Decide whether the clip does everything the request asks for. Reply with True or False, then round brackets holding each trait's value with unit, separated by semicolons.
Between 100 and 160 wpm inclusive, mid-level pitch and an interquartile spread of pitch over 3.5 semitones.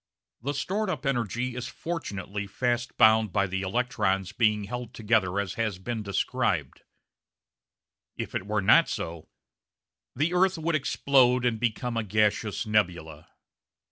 False (140 wpm; 110 Hz; 3.9 semitones)